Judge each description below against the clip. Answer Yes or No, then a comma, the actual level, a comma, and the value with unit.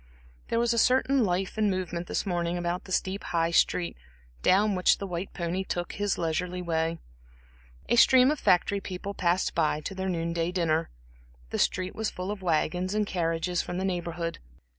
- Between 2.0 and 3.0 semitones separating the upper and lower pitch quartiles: Yes, narrow, 2.5 semitones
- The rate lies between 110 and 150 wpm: No, average, 185 wpm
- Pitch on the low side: No, medium, 180 Hz